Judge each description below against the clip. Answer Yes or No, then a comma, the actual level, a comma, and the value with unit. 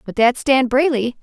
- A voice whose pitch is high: Yes, very high, 255 Hz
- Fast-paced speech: No, average, 195 wpm